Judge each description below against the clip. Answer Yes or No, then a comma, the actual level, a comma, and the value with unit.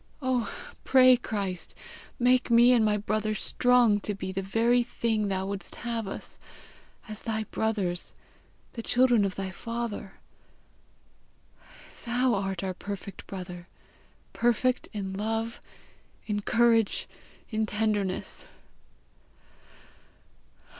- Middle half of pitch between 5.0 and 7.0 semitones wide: No, average, 3.3 semitones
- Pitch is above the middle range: Yes, high, 215 Hz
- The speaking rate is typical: No, slow, 110 wpm